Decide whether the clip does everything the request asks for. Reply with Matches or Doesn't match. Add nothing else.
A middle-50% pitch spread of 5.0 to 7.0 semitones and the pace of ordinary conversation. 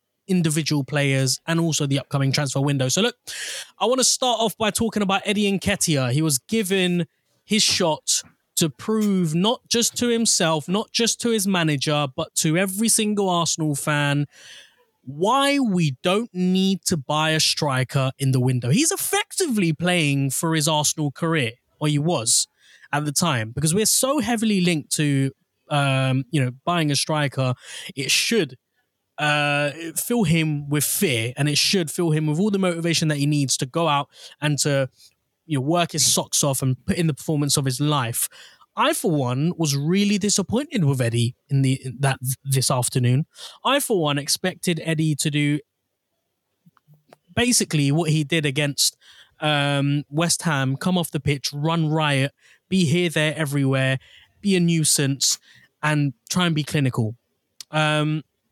Doesn't match